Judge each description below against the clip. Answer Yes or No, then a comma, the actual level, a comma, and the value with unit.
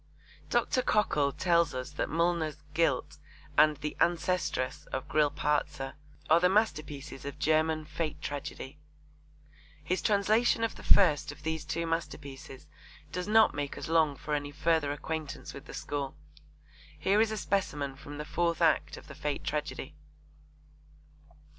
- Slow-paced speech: No, average, 145 wpm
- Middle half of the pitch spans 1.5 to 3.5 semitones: Yes, average, 2.8 semitones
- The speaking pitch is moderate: Yes, medium, 155 Hz